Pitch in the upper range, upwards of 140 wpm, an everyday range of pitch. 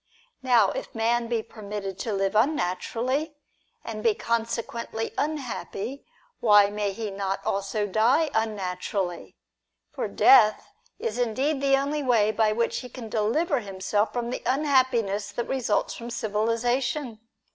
No: high, 230 Hz; slow, 135 wpm; average, 3.6 semitones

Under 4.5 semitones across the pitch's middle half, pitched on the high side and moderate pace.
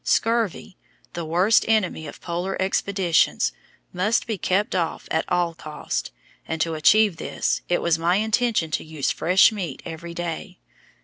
No: average, 3.8 semitones; medium, 175 Hz; average, 150 wpm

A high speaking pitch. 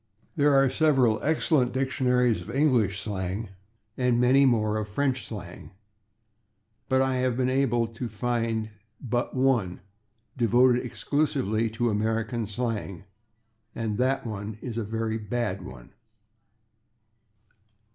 No: low, 120 Hz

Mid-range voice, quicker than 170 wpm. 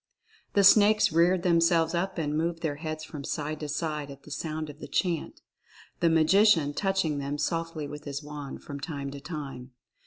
Yes: medium, 155 Hz; average, 185 wpm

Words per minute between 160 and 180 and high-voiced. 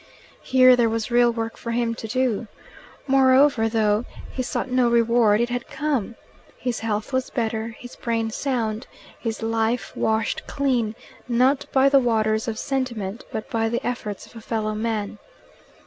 Yes: average, 165 wpm; high, 230 Hz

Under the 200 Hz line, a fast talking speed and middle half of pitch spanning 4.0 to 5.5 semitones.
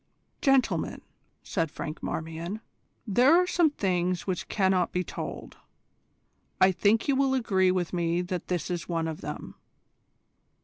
No: medium, 185 Hz; average, 140 wpm; average, 4.6 semitones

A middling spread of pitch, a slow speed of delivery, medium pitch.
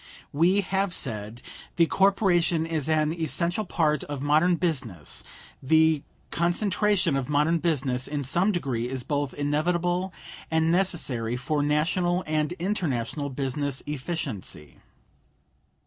Yes: average, 4.1 semitones; slow, 115 wpm; medium, 155 Hz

